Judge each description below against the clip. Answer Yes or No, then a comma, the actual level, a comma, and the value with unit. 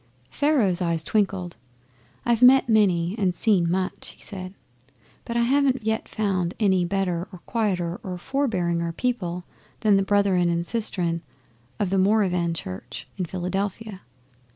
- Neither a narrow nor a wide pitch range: Yes, average, 3.7 semitones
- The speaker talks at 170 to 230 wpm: No, average, 140 wpm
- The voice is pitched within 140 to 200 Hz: Yes, high, 190 Hz